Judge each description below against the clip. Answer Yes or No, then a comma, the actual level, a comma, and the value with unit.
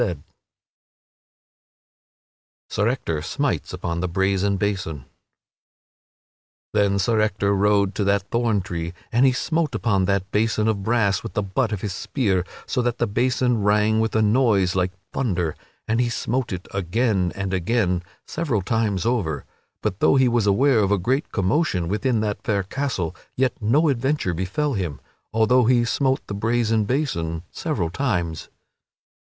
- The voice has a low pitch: Yes, low, 105 Hz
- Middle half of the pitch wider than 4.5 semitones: No, average, 4.2 semitones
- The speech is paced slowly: No, average, 155 wpm